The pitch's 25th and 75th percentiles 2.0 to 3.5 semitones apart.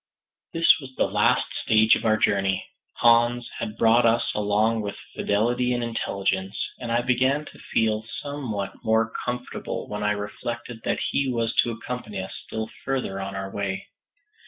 Yes: average, 2.9 semitones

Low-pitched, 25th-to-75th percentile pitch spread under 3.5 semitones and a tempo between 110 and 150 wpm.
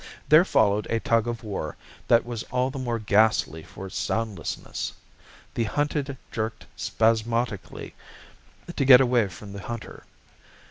Yes: low, 115 Hz; average, 2.9 semitones; average, 140 wpm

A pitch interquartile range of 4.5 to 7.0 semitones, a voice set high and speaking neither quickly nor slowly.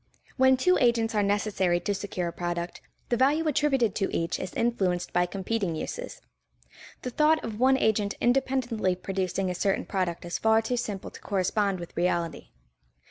Yes: average, 4.9 semitones; high, 205 Hz; average, 170 wpm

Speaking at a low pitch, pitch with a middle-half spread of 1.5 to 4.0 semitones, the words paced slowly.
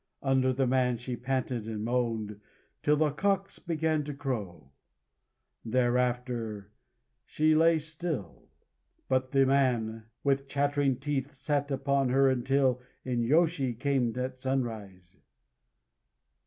Yes: low, 130 Hz; average, 2.9 semitones; slow, 115 wpm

